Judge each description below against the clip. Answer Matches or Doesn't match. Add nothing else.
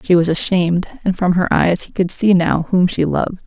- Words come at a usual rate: Doesn't match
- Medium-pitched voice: Matches